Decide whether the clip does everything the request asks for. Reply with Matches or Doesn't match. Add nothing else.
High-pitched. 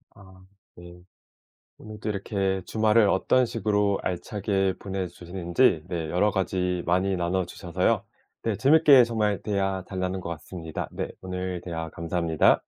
Doesn't match